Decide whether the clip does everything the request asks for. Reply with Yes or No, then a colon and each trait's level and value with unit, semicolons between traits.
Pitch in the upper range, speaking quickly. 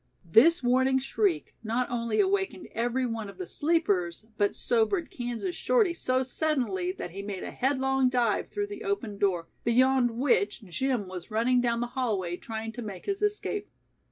No: high, 240 Hz; average, 170 wpm